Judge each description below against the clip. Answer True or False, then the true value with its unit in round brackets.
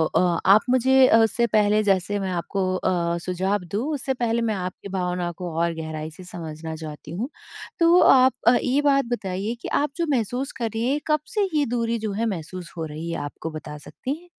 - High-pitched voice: True (200 Hz)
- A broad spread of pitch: True (6.1 semitones)